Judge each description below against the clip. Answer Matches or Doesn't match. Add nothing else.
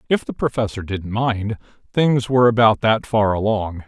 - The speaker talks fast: Doesn't match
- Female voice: Doesn't match